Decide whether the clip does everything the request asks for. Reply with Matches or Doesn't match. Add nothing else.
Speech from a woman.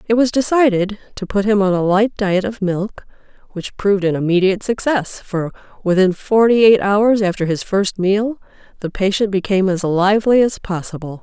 Matches